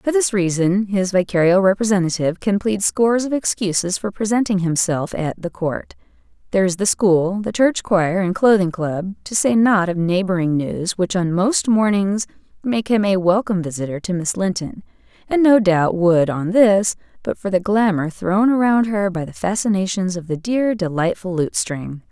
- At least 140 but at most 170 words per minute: No, average, 180 wpm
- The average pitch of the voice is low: No, high, 195 Hz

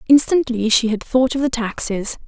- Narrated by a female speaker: Yes, female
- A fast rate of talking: No, average, 185 wpm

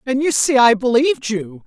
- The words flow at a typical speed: No, fast, 215 wpm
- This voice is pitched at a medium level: No, high, 245 Hz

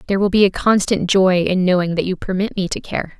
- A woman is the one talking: Yes, female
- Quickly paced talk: Yes, fast, 265 wpm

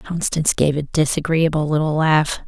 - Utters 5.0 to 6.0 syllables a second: Yes, 5.1 syllables/s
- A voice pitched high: No, medium, 155 Hz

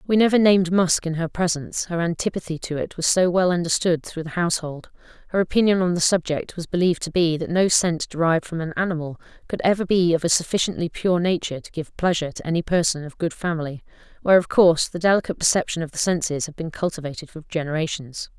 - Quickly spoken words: Yes, fast, 210 wpm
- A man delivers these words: No, female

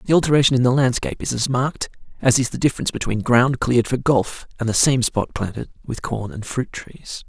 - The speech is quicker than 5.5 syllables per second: Yes, 6.0 syllables/s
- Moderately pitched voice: No, low, 125 Hz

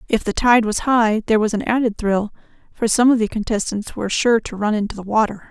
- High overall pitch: Yes, high, 220 Hz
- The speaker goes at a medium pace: No, fast, 240 wpm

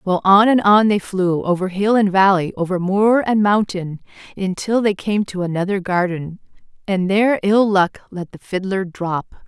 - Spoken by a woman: Yes, female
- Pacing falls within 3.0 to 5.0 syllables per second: Yes, 4.7 syllables/s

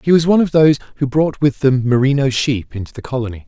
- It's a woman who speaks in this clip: No, male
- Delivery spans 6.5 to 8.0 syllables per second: Yes, 6.7 syllables/s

